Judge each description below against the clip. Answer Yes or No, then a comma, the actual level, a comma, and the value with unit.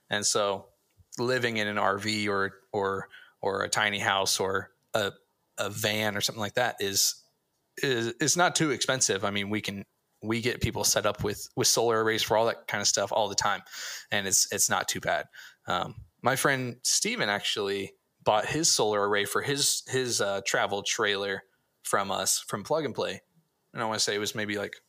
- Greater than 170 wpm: Yes, average, 200 wpm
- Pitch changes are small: No, average, 3.7 semitones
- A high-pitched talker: No, low, 105 Hz